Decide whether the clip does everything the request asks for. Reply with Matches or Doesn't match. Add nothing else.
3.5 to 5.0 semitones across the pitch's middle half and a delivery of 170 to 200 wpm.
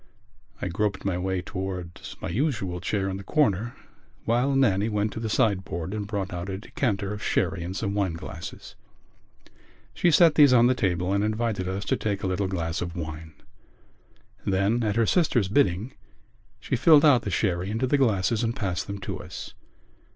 Matches